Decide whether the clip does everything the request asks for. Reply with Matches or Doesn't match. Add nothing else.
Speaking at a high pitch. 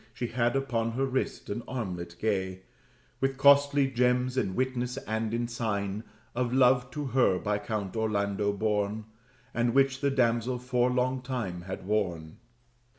Doesn't match